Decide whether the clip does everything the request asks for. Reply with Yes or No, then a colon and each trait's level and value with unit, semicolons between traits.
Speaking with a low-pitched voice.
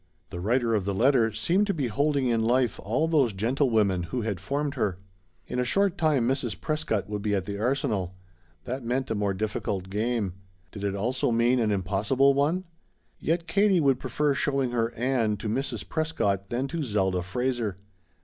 Yes: low, 120 Hz